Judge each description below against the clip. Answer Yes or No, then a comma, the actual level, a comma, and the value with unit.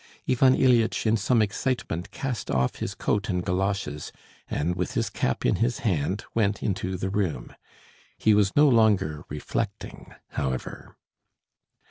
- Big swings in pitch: No, average, 4.6 semitones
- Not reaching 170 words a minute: Yes, average, 140 wpm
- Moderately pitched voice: No, low, 100 Hz